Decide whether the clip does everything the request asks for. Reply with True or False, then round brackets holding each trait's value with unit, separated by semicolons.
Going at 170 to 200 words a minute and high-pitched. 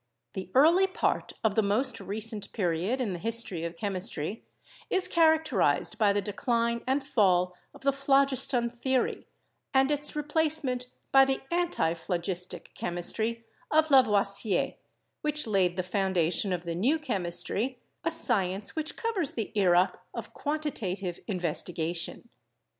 False (135 wpm; 220 Hz)